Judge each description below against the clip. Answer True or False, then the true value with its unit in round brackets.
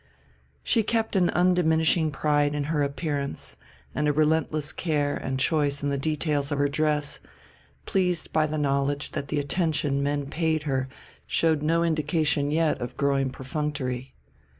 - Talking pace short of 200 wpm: True (150 wpm)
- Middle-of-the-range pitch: True (150 Hz)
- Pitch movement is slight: True (2.1 semitones)